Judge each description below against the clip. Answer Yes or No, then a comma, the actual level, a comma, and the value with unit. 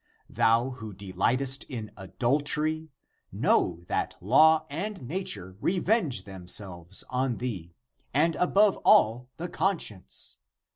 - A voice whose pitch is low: Yes, low, 125 Hz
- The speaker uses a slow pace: Yes, slow, 110 wpm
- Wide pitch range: Yes, wide, 7.9 semitones